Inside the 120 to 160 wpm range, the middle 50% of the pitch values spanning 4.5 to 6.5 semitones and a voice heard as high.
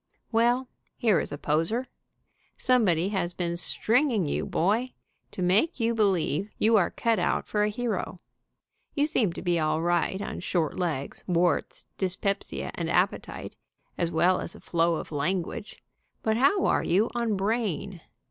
Yes: average, 155 wpm; average, 4.8 semitones; high, 195 Hz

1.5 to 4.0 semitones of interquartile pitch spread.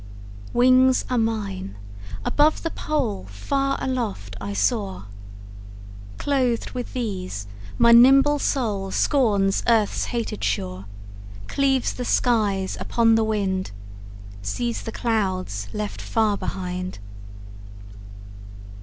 No: average, 5.0 semitones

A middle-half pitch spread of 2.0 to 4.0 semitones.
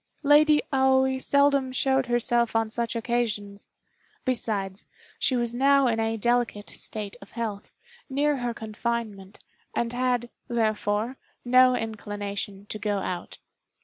Yes: average, 3.5 semitones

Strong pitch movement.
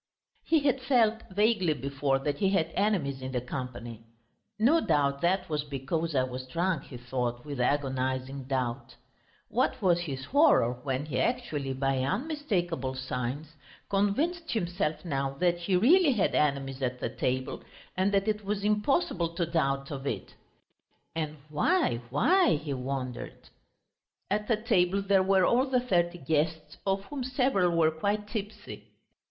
Yes: wide, 7.4 semitones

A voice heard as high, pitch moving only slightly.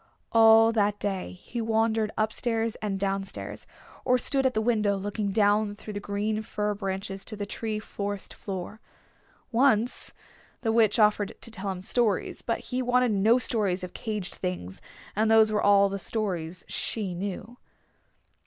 Yes: high, 210 Hz; narrow, 2.2 semitones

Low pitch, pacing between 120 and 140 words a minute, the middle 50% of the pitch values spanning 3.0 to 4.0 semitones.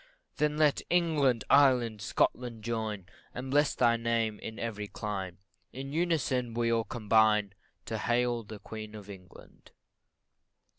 Yes: low, 115 Hz; slow, 135 wpm; average, 3.4 semitones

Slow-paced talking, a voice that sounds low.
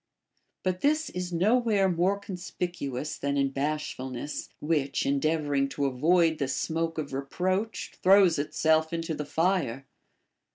No: slow, 130 wpm; medium, 160 Hz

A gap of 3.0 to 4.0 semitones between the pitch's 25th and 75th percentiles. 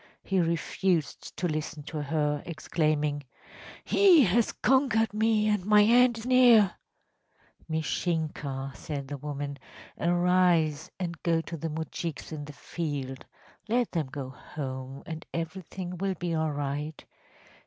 No: average, 4.5 semitones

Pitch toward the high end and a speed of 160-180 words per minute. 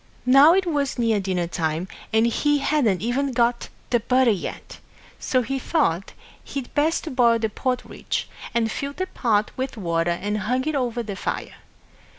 Yes: high, 240 Hz; average, 165 wpm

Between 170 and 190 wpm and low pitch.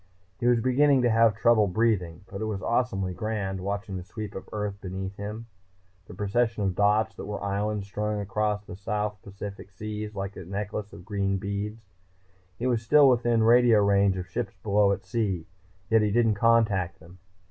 Yes: average, 185 wpm; low, 105 Hz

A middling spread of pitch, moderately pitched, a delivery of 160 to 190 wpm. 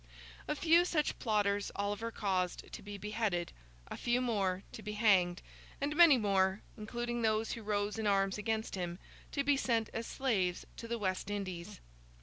No: average, 3.1 semitones; high, 210 Hz; average, 170 wpm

